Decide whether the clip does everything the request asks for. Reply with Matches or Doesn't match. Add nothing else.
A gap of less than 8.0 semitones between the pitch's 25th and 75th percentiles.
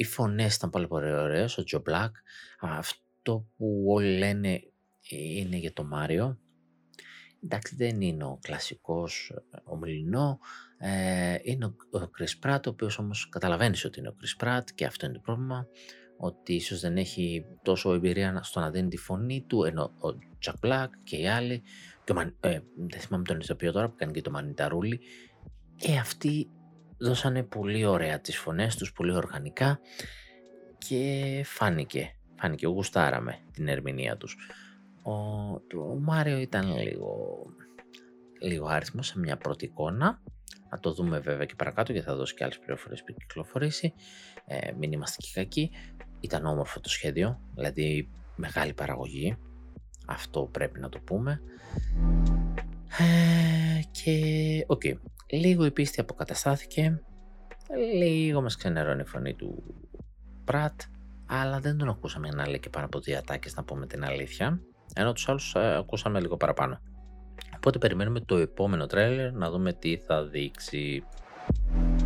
Doesn't match